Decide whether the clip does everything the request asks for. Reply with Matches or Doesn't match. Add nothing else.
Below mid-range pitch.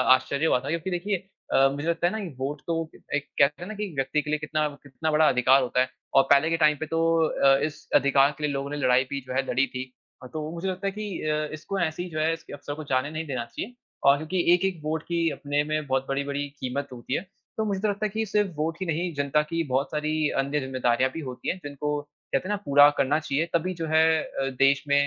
Doesn't match